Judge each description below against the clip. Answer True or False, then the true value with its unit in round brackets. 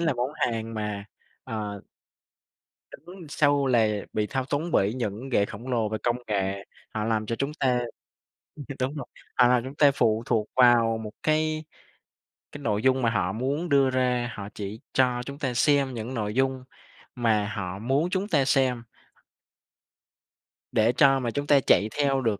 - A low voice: True (125 Hz)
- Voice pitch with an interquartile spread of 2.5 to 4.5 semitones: True (4.0 semitones)